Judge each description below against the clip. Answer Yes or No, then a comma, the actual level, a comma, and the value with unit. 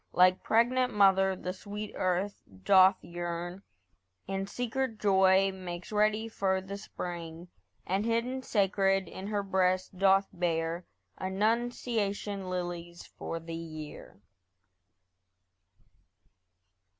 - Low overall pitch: No, high, 190 Hz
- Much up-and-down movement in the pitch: No, narrow, 2.6 semitones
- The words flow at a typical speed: No, slow, 100 wpm